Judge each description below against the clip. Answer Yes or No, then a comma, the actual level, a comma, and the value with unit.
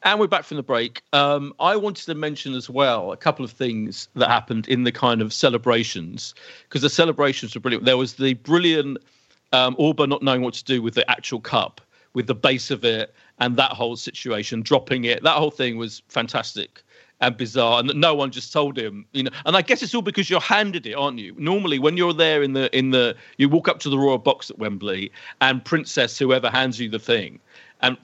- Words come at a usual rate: No, fast, 230 wpm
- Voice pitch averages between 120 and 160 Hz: Yes, low, 130 Hz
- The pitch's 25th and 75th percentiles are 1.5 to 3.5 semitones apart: No, average, 3.9 semitones